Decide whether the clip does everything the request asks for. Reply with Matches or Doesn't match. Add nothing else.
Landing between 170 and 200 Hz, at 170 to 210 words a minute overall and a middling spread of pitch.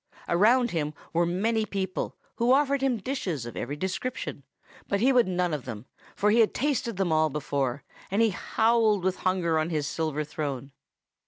Doesn't match